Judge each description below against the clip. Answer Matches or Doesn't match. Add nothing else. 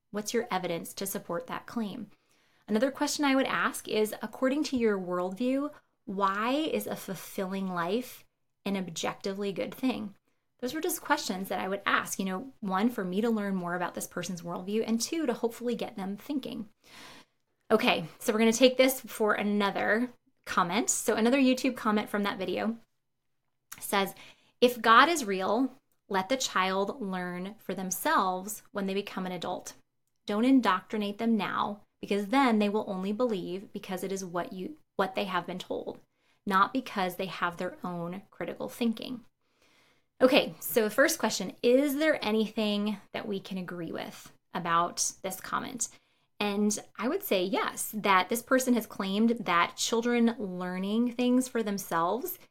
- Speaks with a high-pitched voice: Matches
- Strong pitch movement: Doesn't match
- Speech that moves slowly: Doesn't match